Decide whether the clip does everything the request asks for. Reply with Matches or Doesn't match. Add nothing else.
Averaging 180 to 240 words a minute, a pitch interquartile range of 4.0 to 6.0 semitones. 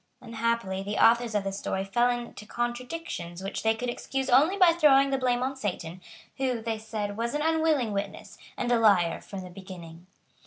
Matches